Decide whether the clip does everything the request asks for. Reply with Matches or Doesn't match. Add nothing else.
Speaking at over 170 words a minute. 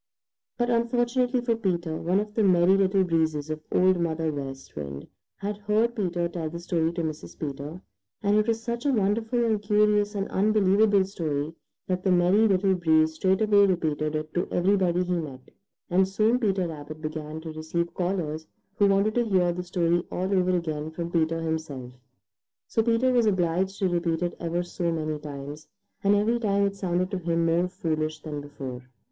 Matches